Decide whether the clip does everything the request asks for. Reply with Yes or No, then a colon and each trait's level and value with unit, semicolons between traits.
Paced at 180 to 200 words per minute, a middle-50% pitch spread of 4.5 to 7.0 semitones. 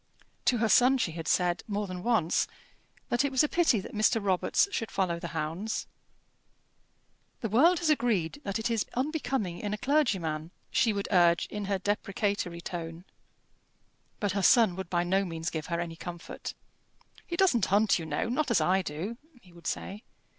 Yes: average, 185 wpm; wide, 5.4 semitones